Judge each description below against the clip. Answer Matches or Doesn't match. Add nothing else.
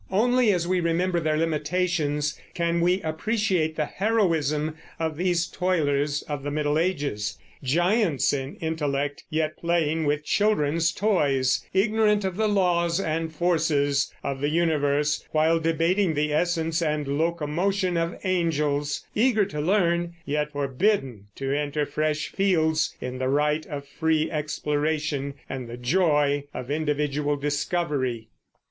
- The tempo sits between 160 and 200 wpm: Doesn't match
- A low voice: Doesn't match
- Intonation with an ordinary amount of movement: Matches